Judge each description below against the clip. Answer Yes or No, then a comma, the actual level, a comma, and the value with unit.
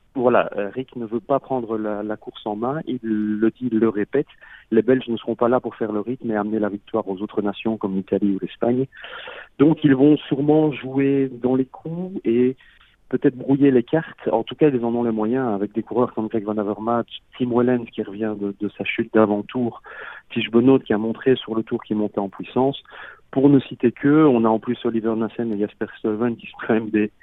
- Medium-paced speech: No, fast, 230 wpm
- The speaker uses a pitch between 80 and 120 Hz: Yes, low, 115 Hz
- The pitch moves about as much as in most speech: Yes, average, 3.2 semitones